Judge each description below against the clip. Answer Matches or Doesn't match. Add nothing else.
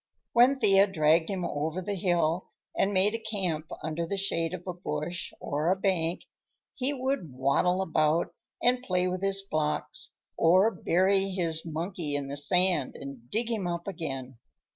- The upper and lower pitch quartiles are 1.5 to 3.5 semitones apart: Doesn't match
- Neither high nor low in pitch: Matches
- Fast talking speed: Doesn't match